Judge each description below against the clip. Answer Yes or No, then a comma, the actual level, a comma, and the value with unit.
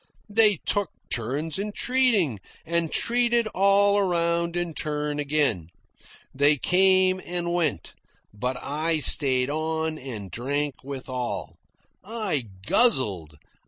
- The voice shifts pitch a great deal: Yes, wide, 6.0 semitones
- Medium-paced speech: No, slow, 115 wpm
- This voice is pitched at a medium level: Yes, medium, 160 Hz